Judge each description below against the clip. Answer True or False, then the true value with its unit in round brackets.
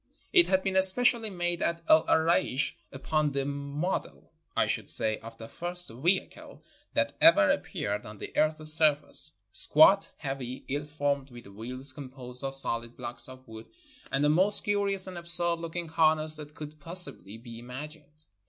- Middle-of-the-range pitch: True (150 Hz)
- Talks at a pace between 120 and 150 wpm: False (170 wpm)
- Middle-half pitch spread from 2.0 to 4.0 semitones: False (5.1 semitones)